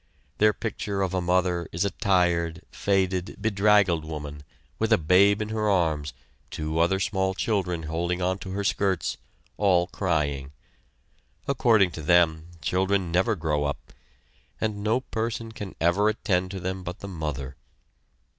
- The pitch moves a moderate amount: Yes, average, 3.5 semitones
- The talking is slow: No, average, 145 wpm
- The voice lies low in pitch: Yes, very low, 95 Hz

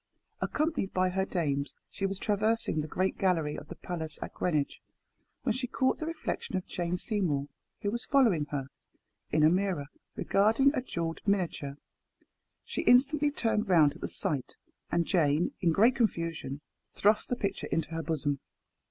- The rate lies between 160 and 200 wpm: Yes, average, 165 wpm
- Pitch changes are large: Yes, wide, 5.8 semitones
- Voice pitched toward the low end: No, medium, 185 Hz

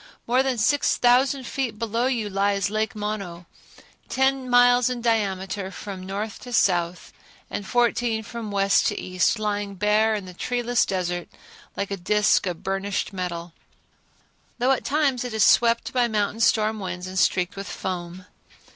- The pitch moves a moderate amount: Yes, average, 4.0 semitones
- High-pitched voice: Yes, high, 210 Hz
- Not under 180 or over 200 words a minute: No, average, 160 wpm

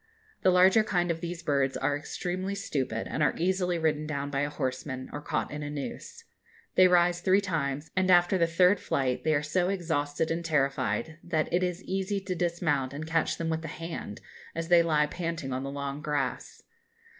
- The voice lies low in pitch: No, medium, 165 Hz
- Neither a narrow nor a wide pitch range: Yes, average, 3.6 semitones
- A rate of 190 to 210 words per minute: Yes, average, 200 wpm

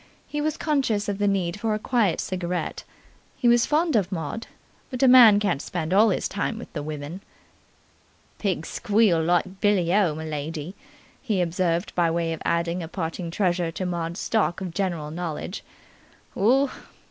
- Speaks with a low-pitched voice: No, medium, 185 Hz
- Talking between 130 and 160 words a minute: No, average, 170 wpm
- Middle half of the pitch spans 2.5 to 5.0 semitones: Yes, average, 4.1 semitones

